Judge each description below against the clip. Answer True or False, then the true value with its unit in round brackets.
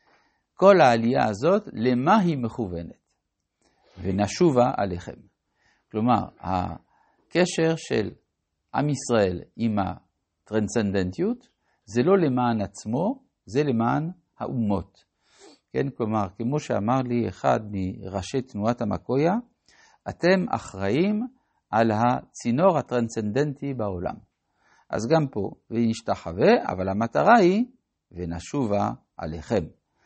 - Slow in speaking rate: True (95 wpm)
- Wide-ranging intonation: True (8.0 semitones)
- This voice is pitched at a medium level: False (120 Hz)